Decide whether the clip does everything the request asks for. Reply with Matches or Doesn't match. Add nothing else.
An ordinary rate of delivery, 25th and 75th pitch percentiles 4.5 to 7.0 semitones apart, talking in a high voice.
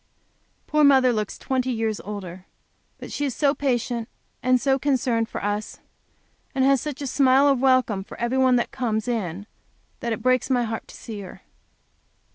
Doesn't match